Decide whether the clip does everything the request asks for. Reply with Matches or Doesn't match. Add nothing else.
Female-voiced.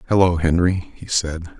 Doesn't match